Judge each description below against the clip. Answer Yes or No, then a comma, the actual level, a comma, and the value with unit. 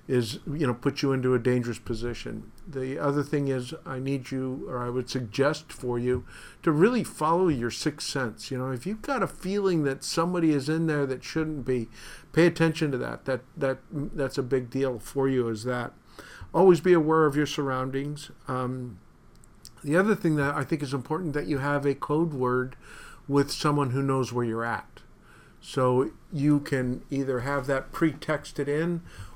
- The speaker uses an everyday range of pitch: Yes, average, 3.4 semitones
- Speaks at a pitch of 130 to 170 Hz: Yes, medium, 140 Hz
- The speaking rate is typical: Yes, average, 190 wpm